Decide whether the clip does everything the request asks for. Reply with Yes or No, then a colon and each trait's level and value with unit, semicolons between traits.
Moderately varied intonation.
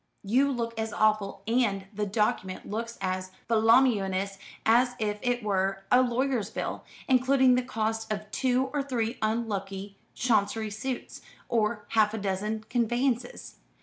Yes: average, 3.1 semitones